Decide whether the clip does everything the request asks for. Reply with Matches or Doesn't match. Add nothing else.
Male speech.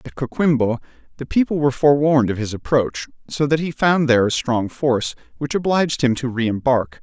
Matches